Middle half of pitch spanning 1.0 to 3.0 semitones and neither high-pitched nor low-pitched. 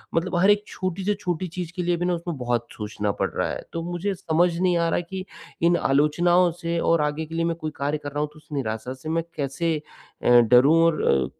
No: average, 3.4 semitones; medium, 165 Hz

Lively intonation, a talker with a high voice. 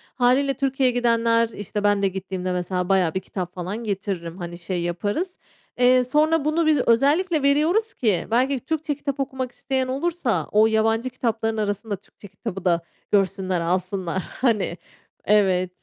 Yes: wide, 6.0 semitones; high, 225 Hz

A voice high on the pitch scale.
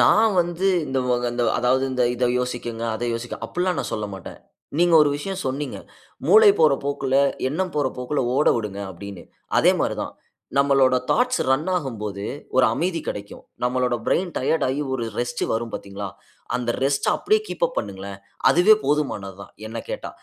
No: low, 130 Hz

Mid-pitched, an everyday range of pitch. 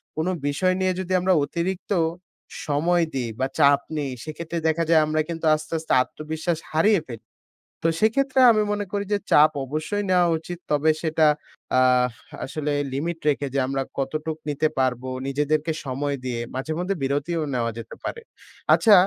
Yes: medium, 155 Hz; average, 3.7 semitones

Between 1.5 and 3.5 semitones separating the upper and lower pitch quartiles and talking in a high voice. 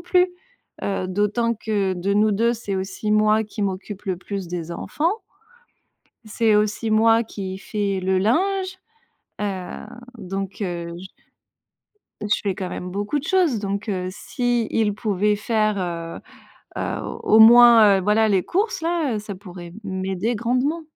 Yes: average, 3.0 semitones; high, 210 Hz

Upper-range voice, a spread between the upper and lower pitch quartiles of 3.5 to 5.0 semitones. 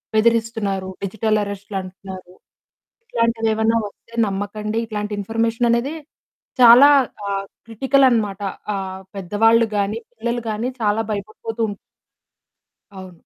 No: high, 215 Hz; narrow, 2.5 semitones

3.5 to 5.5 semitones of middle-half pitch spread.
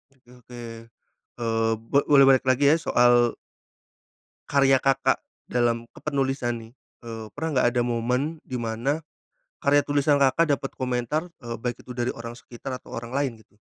No: average, 2.8 semitones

